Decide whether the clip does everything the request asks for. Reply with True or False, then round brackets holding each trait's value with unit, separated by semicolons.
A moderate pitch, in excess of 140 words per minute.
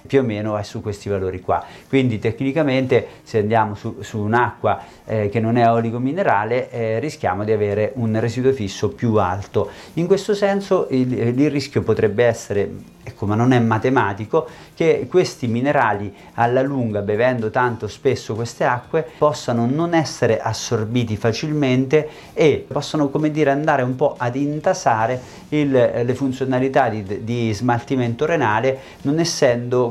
False (125 Hz; 150 wpm)